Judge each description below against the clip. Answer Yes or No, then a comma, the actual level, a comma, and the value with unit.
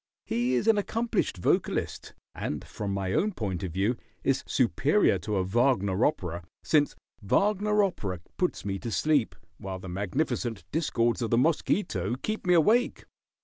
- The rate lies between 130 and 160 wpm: Yes, average, 155 wpm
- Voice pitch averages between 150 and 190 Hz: No, low, 120 Hz